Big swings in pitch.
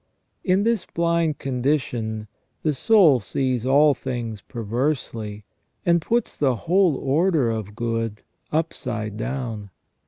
Yes: wide, 5.9 semitones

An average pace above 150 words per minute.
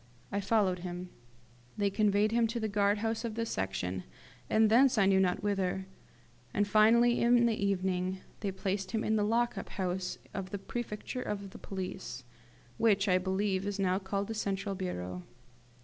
Yes: average, 170 wpm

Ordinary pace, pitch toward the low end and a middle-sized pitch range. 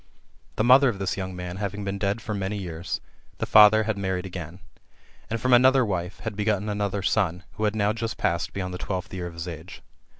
No: fast, 220 wpm; low, 100 Hz; average, 3.0 semitones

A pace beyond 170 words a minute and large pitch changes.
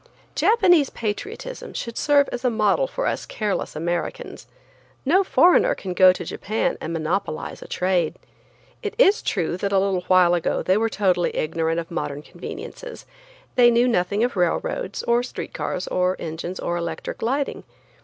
No: average, 165 wpm; wide, 7.3 semitones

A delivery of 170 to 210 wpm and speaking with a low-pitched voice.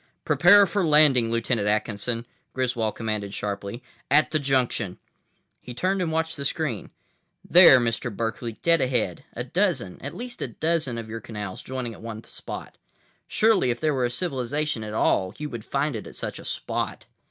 Yes: average, 175 wpm; low, 125 Hz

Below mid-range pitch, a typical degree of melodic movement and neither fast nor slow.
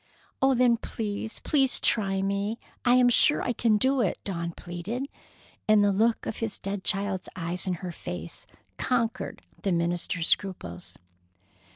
No: high, 205 Hz; average, 4.4 semitones; average, 155 wpm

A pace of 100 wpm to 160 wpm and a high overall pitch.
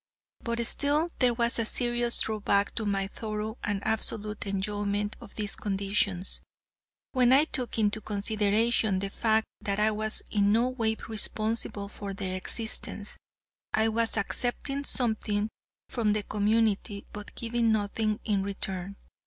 Yes: average, 140 wpm; high, 215 Hz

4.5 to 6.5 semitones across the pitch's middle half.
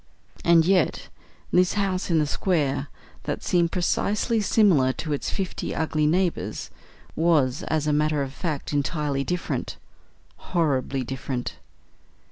No: average, 4.0 semitones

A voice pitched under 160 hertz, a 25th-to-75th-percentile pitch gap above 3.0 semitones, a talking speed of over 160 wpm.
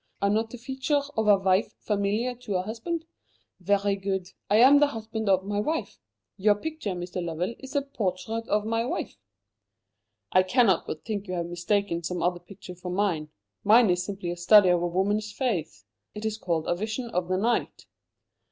No: high, 205 Hz; average, 3.8 semitones; average, 190 wpm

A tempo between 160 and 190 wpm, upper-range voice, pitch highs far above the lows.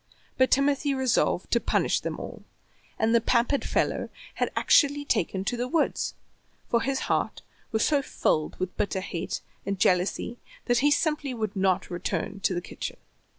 Yes: average, 165 wpm; high, 235 Hz; wide, 6.3 semitones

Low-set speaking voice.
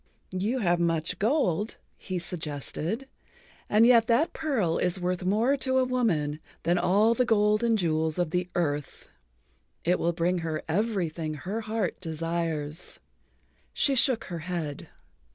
No: medium, 180 Hz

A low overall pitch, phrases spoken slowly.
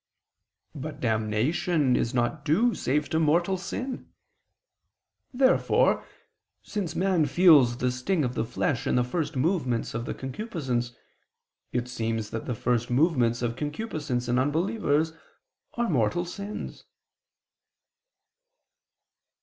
No: medium, 145 Hz; slow, 115 wpm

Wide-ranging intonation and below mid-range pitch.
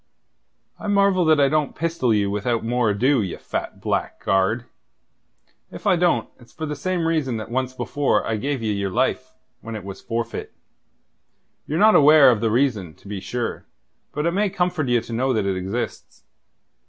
Yes: wide, 6.1 semitones; low, 125 Hz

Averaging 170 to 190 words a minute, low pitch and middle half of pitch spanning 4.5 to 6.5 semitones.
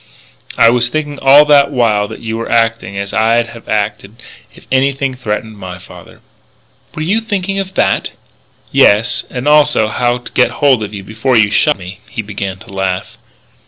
Yes: average, 180 wpm; low, 115 Hz; average, 4.8 semitones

